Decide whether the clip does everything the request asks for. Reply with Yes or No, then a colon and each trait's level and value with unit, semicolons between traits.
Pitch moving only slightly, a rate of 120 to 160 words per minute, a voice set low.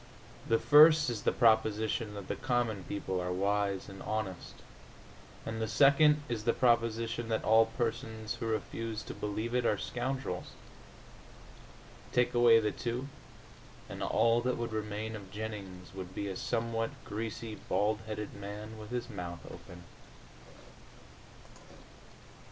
Yes: narrow, 2.3 semitones; average, 140 wpm; low, 110 Hz